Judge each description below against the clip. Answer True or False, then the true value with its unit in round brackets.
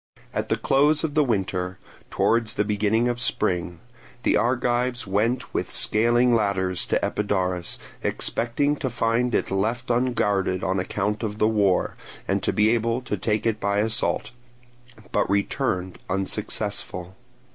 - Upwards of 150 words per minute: False (145 wpm)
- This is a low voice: True (110 Hz)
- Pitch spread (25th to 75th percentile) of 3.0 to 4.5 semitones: True (3.7 semitones)